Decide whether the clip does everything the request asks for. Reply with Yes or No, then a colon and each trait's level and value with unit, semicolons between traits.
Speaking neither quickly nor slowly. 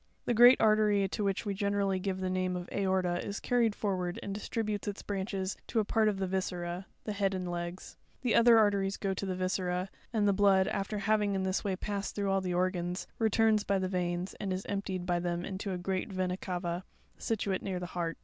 No: fast, 220 wpm